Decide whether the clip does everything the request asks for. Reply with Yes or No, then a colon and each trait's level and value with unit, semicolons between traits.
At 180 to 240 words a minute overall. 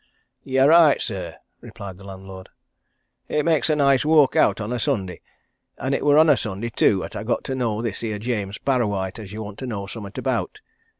Yes: fast, 205 wpm